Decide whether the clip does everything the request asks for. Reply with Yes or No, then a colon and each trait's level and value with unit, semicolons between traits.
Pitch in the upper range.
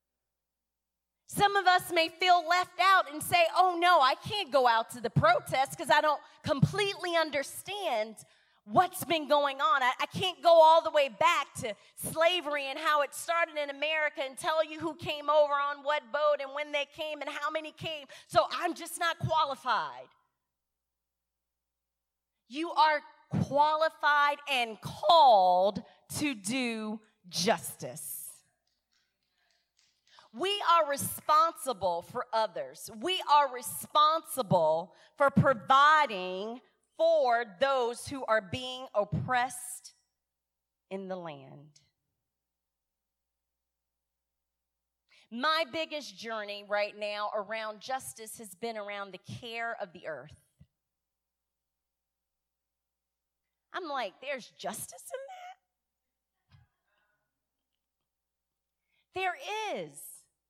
Yes: very high, 250 Hz